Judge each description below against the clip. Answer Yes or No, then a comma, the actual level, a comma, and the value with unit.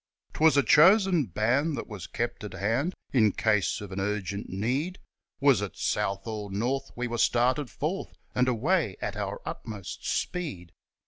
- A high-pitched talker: No, low, 115 Hz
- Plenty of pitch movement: Yes, wide, 5.8 semitones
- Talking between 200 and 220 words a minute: No, average, 160 wpm